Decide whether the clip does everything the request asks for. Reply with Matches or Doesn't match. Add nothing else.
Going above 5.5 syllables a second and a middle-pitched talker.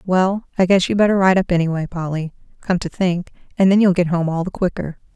Matches